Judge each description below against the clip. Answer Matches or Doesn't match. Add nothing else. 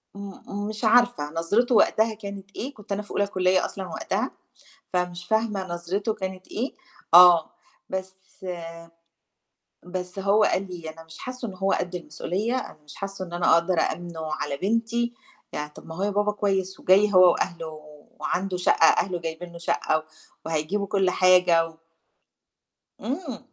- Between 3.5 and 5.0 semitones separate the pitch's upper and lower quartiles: Doesn't match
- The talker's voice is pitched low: Doesn't match